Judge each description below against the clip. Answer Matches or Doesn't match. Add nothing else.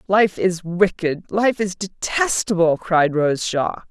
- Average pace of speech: Doesn't match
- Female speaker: Matches